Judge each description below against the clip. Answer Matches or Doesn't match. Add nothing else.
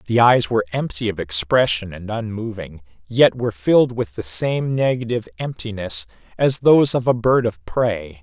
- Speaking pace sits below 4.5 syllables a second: Doesn't match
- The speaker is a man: Matches